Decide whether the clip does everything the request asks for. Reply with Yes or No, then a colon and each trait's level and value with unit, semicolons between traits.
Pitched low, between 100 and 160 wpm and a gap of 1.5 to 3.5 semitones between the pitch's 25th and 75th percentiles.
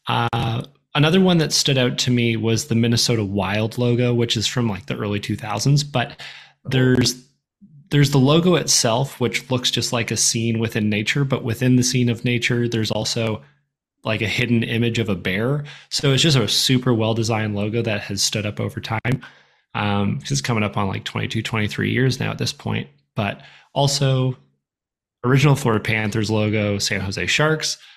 No: low, 120 Hz; average, 180 wpm; average, 3.2 semitones